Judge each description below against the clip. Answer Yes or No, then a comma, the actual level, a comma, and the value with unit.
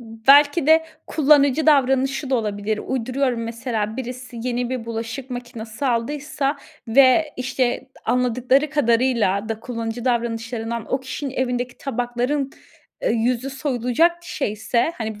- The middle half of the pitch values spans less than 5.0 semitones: Yes, average, 2.9 semitones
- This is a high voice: Yes, very high, 250 Hz